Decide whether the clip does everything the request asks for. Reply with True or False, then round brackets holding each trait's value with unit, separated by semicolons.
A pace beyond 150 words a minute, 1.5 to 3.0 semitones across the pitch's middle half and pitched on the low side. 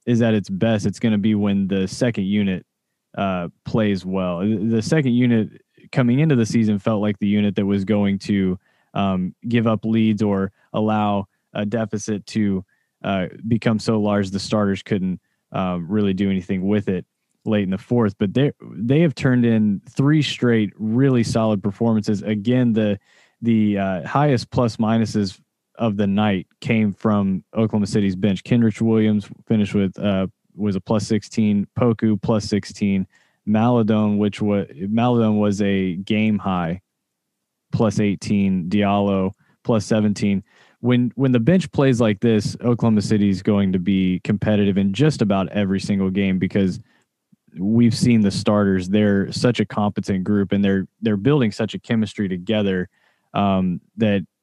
True (160 wpm; 2.4 semitones; 105 Hz)